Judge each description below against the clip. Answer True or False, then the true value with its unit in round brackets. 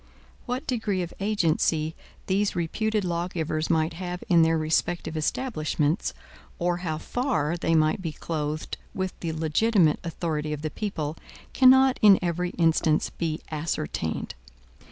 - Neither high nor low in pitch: True (170 Hz)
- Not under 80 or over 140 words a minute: True (135 wpm)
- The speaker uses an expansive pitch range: False (3.4 semitones)